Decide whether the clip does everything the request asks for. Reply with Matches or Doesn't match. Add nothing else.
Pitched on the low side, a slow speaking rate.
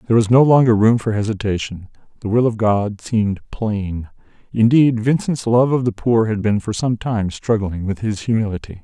Doesn't match